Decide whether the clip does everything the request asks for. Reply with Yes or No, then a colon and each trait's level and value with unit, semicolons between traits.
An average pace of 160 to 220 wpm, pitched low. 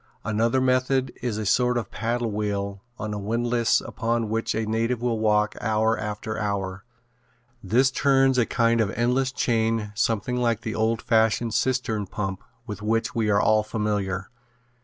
Yes: average, 170 wpm; low, 110 Hz